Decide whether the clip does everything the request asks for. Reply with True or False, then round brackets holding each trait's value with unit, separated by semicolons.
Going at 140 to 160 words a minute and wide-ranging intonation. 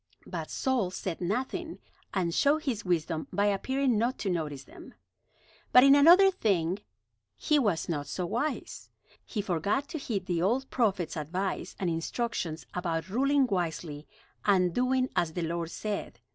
True (155 wpm; 7.2 semitones)